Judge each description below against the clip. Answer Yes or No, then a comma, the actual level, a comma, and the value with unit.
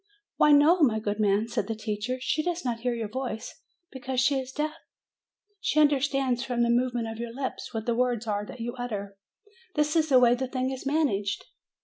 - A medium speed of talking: No, fast, 210 wpm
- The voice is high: Yes, high, 245 Hz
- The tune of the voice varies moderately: Yes, average, 3.2 semitones